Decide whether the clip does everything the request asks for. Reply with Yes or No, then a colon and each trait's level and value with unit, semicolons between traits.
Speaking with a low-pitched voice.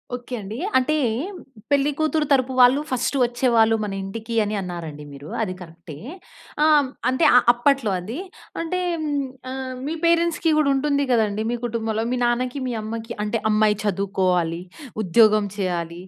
No: high, 230 Hz